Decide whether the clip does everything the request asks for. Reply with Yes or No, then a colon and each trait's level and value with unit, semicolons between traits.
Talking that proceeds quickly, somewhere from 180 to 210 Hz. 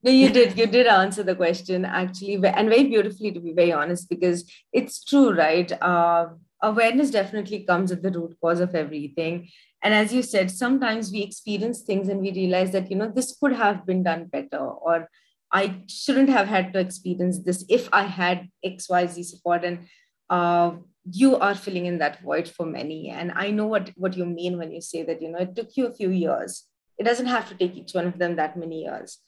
Yes: fast, 215 wpm; medium, 185 Hz